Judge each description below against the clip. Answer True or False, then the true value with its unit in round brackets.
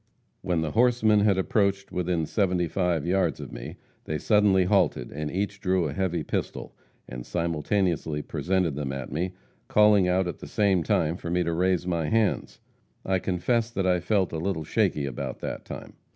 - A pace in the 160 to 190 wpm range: True (180 wpm)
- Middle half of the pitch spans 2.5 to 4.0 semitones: True (3.2 semitones)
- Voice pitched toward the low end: True (90 Hz)